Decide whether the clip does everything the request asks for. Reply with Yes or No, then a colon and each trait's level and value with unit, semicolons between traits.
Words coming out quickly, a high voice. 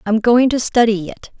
Yes: fast, 215 wpm; high, 235 Hz